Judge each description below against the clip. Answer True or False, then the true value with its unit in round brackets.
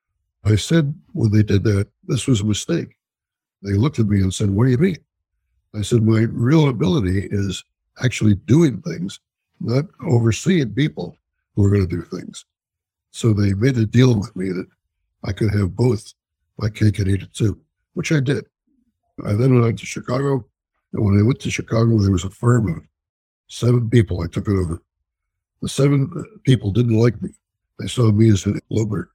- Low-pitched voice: True (110 Hz)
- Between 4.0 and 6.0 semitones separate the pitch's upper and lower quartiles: True (4.5 semitones)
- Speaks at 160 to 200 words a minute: True (195 wpm)